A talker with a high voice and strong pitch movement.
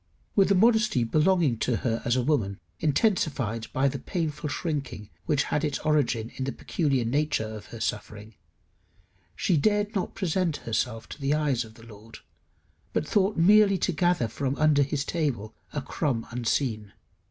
No: medium, 140 Hz; wide, 6.3 semitones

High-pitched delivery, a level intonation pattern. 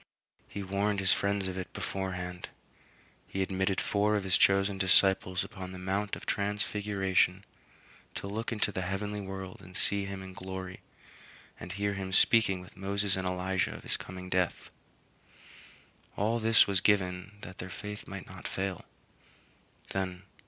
No: very low, 95 Hz; narrow, 1.5 semitones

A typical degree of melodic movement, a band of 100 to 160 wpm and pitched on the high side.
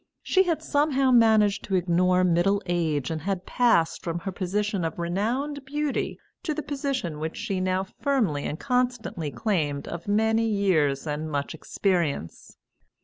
No: wide, 6.6 semitones; average, 150 wpm; high, 195 Hz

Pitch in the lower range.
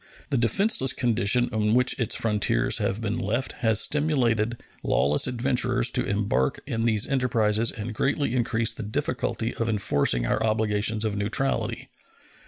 Yes: low, 115 Hz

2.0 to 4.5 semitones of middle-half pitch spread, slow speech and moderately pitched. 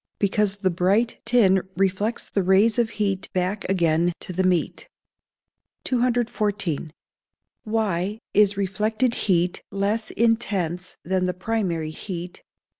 No: average, 3.0 semitones; slow, 120 wpm; high, 195 Hz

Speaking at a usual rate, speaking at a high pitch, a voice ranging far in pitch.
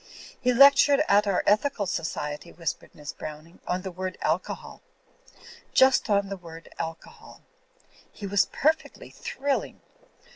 No: slow, 125 wpm; high, 195 Hz; wide, 7.0 semitones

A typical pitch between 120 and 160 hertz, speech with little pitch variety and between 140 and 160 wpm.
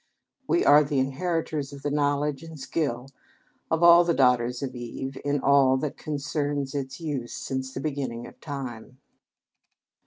Yes: medium, 140 Hz; narrow, 2.2 semitones; average, 155 wpm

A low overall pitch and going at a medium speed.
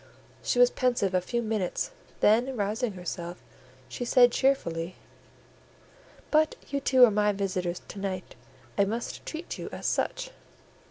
No: high, 215 Hz; average, 145 wpm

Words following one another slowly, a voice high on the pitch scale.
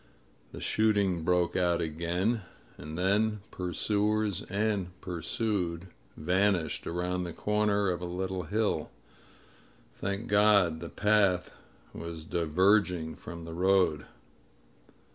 No: slow, 110 wpm; very low, 90 Hz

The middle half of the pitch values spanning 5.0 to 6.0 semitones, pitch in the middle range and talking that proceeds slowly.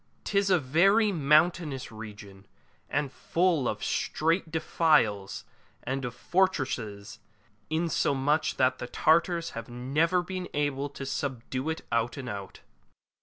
Yes: wide, 5.5 semitones; medium, 145 Hz; slow, 125 wpm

